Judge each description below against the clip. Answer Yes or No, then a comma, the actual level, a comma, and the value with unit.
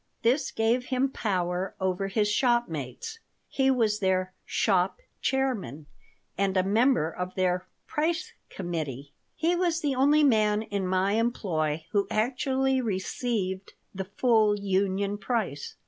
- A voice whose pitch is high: Yes, high, 205 Hz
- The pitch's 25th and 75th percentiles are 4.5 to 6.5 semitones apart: Yes, average, 5.2 semitones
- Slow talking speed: Yes, slow, 130 wpm